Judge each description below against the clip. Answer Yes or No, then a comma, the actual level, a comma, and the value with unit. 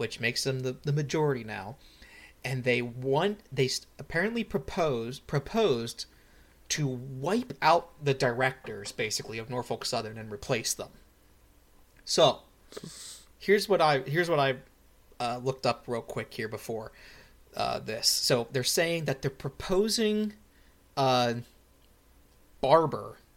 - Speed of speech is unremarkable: No, slow, 125 wpm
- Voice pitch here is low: Yes, low, 130 Hz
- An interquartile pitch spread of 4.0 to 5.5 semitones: Yes, average, 4.7 semitones